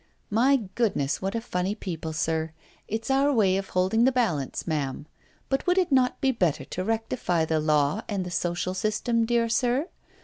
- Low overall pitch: No, high, 205 Hz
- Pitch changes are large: Yes, wide, 6.1 semitones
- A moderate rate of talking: Yes, average, 190 wpm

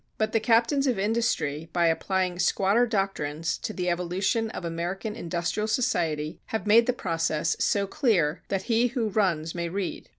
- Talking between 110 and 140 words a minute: No, average, 165 wpm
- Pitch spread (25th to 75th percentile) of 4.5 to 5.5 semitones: Yes, average, 4.8 semitones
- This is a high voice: Yes, high, 195 Hz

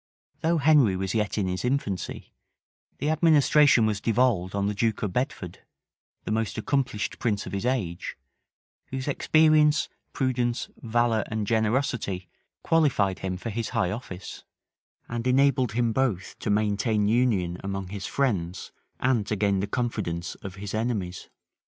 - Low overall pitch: Yes, low, 110 Hz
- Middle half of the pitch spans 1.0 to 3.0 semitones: No, average, 4.6 semitones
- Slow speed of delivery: No, average, 145 wpm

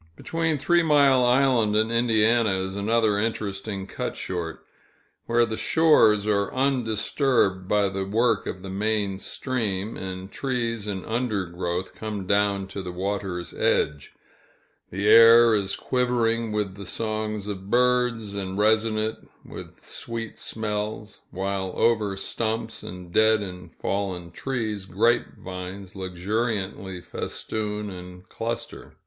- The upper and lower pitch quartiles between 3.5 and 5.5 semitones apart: No, average, 3.1 semitones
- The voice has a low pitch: Yes, low, 105 Hz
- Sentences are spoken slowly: Yes, slow, 125 wpm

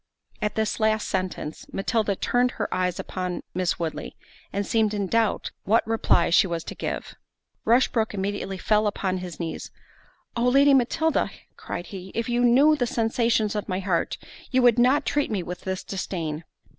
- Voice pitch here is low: No, high, 210 Hz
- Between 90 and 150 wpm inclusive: No, average, 170 wpm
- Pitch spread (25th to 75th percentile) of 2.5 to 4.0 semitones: No, average, 4.4 semitones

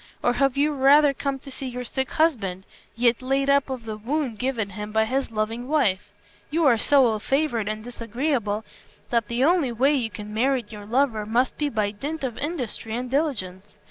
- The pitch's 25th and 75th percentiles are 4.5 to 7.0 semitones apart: No, average, 4.0 semitones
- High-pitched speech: Yes, high, 245 Hz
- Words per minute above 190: Yes, average, 200 wpm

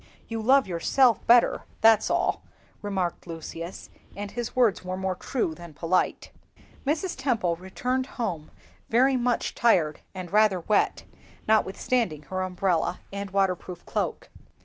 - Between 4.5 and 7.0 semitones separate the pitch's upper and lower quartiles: Yes, average, 5.0 semitones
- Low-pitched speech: No, high, 195 Hz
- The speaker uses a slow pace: Yes, slow, 130 wpm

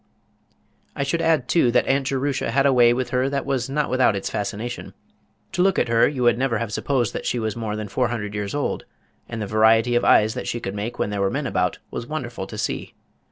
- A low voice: Yes, low, 120 Hz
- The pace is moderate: No, fast, 245 wpm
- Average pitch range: Yes, average, 3.7 semitones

